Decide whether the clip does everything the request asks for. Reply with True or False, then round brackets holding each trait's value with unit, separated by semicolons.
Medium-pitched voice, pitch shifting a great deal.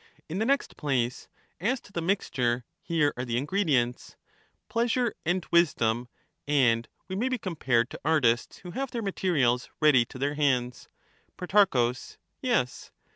True (150 Hz; 7.8 semitones)